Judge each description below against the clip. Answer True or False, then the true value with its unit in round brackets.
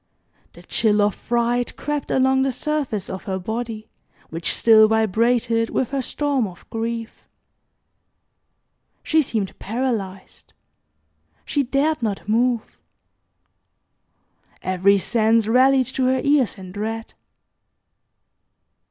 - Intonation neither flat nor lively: True (3.5 semitones)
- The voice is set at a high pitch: True (230 Hz)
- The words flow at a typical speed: False (110 wpm)